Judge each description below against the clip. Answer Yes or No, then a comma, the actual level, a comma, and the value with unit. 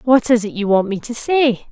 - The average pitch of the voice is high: Yes, high, 235 Hz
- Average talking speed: No, fast, 280 wpm